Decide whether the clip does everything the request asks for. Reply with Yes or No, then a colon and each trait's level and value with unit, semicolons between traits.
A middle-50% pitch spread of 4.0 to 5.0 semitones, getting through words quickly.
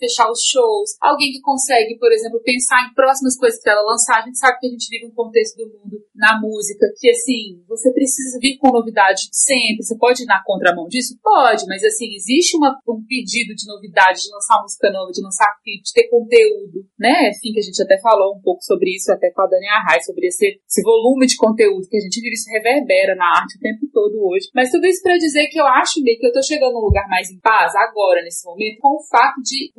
Yes: average, 4.7 semitones; fast, 240 wpm